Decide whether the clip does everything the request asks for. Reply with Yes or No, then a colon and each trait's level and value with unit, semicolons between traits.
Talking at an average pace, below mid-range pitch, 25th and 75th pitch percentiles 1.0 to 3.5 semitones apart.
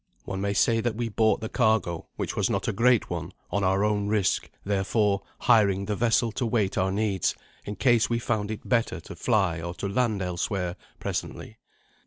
Yes: average, 195 wpm; low, 105 Hz; average, 2.9 semitones